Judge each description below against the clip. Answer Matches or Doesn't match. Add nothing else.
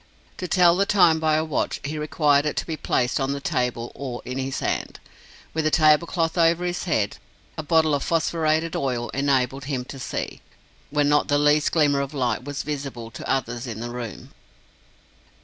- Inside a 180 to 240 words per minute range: Matches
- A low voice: Doesn't match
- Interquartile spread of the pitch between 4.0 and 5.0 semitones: Doesn't match